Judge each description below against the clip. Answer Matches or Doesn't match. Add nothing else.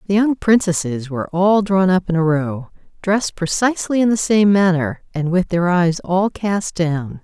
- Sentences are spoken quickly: Doesn't match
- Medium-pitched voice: Matches